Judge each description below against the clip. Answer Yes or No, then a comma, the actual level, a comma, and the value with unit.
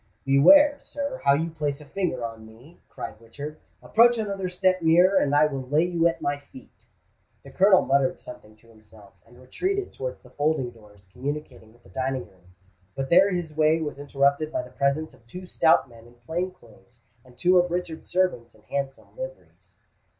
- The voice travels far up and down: Yes, wide, 6.3 semitones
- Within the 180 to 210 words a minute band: Yes, average, 190 wpm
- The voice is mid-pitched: Yes, medium, 145 Hz